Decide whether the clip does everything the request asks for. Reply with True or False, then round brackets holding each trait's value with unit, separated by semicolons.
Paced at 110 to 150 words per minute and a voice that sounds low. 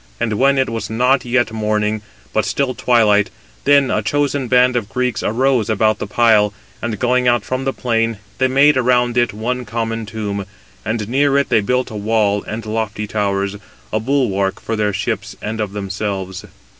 False (180 wpm; 115 Hz)